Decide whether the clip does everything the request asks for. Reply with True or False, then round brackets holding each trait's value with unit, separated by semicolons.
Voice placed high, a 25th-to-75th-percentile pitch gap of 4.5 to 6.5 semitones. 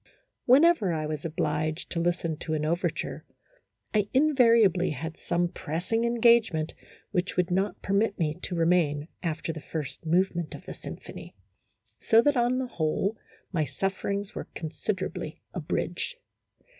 False (175 Hz; 5.0 semitones)